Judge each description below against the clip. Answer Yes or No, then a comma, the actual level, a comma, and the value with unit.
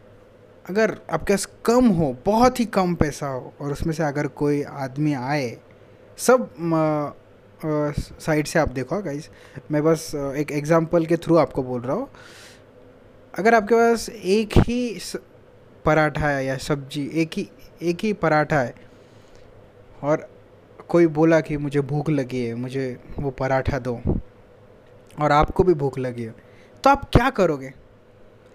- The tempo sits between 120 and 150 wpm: Yes, average, 145 wpm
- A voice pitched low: No, medium, 150 Hz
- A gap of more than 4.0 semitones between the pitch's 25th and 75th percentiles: Yes, average, 4.8 semitones